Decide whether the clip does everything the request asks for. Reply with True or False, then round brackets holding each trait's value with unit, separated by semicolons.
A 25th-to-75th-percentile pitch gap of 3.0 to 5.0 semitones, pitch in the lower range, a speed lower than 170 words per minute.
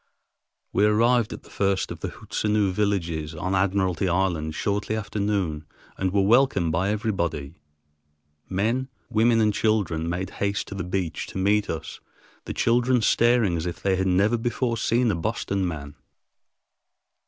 True (3.5 semitones; 100 Hz; 155 wpm)